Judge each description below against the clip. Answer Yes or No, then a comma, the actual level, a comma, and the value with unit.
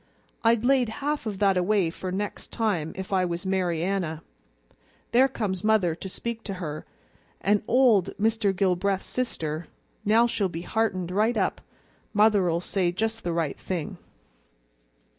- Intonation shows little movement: No, average, 3.9 semitones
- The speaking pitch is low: No, high, 195 Hz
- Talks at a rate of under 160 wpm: Yes, average, 150 wpm